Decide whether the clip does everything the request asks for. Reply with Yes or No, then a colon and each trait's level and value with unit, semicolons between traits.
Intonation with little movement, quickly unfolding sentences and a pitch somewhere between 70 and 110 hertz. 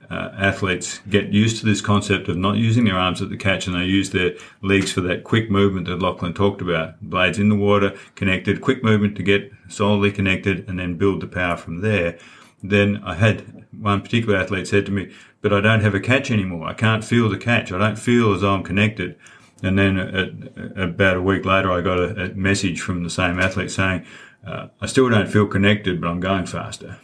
Yes: narrow, 2.1 semitones; fast, 225 wpm; low, 100 Hz